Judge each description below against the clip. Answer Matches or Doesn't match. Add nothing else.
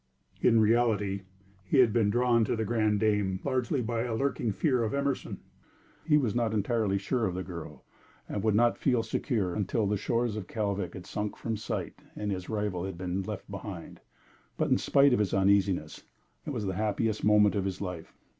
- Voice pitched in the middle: Doesn't match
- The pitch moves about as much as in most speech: Matches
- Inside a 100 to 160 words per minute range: Doesn't match